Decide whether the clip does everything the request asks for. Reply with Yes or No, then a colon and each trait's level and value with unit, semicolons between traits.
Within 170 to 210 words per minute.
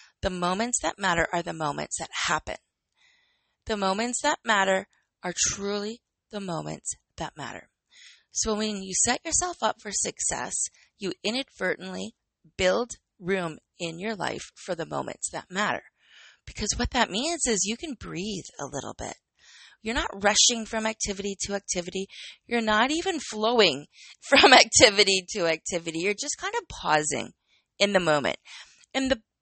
No: average, 155 wpm